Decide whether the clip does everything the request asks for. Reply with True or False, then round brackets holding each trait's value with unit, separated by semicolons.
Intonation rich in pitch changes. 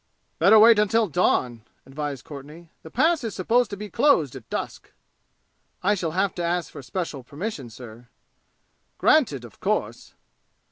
True (7.6 semitones)